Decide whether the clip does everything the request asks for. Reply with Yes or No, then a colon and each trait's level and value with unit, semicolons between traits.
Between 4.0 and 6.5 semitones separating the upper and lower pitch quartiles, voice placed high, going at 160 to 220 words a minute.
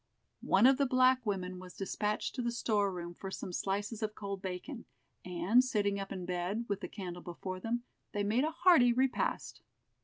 Yes: average, 4.5 semitones; high, 205 Hz; average, 190 wpm